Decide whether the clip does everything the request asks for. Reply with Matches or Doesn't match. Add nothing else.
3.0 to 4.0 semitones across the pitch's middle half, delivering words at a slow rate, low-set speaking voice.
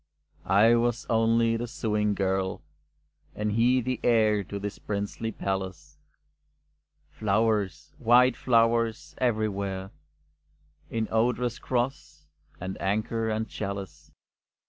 Doesn't match